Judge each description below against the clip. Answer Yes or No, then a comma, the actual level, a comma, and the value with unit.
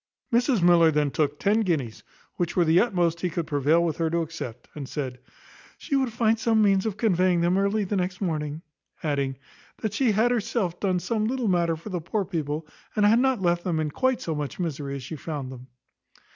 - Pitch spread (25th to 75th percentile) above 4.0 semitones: Yes, wide, 5.4 semitones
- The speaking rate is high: Yes, fast, 215 wpm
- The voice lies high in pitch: No, medium, 175 Hz